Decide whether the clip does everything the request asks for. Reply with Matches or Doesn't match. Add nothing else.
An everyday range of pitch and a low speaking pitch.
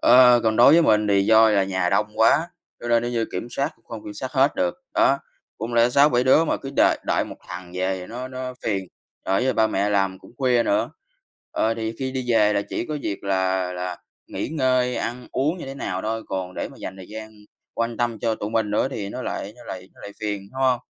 Matches